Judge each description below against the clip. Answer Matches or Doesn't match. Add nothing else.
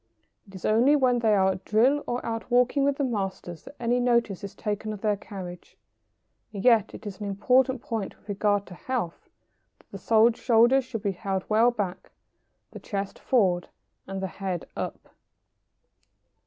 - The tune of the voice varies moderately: Matches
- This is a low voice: Doesn't match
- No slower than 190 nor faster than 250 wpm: Doesn't match